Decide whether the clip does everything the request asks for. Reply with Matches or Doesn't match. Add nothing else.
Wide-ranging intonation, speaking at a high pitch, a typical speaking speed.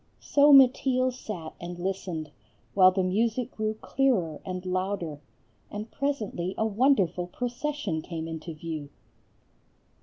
Doesn't match